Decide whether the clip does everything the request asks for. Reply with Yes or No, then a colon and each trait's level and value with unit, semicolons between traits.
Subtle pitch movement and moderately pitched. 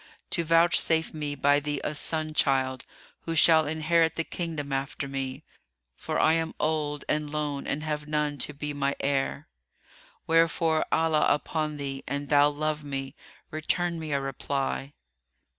Yes: narrow, 2.1 semitones; medium, 150 Hz